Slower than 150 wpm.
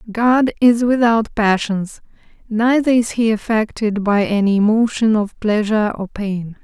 Yes: slow, 135 wpm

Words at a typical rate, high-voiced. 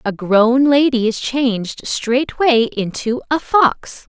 No: slow, 130 wpm; high, 245 Hz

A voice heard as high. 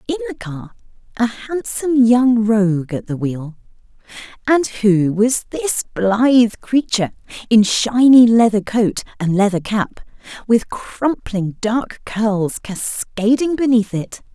Yes: high, 225 Hz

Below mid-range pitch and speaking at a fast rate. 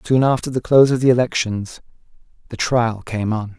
No: low, 120 Hz; average, 185 wpm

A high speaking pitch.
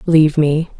No: medium, 155 Hz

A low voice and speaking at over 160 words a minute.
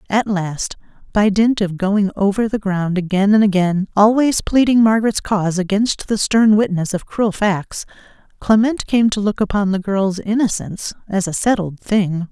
No: high, 200 Hz; average, 170 wpm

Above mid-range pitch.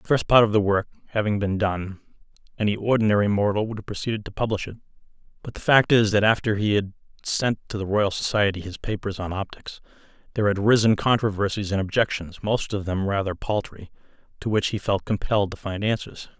No: low, 105 Hz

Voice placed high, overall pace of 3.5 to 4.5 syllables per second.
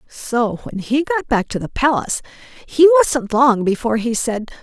Yes: very high, 250 Hz; 4.4 syllables/s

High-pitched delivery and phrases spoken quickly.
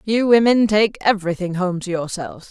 No: high, 200 Hz; average, 170 wpm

